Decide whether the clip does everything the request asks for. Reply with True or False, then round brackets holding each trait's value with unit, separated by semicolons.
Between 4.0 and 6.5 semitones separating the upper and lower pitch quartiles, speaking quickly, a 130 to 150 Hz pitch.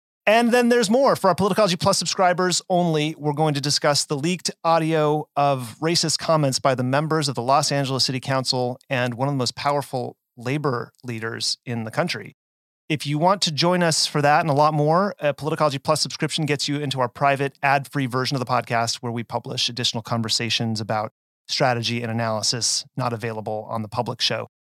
False (4.4 semitones; 195 wpm; 140 Hz)